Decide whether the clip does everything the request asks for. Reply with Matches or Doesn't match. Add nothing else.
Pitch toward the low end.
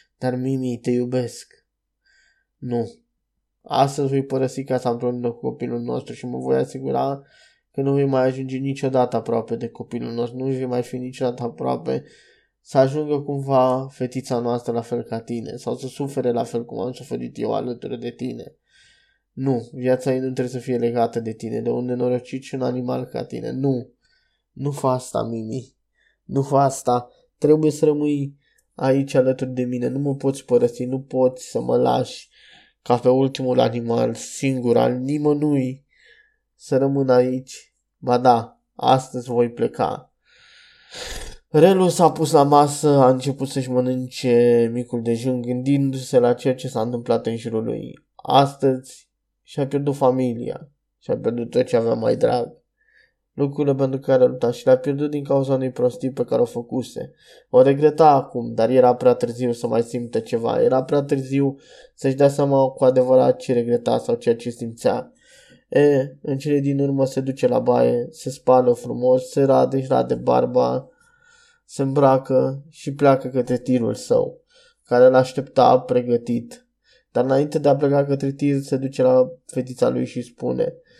Matches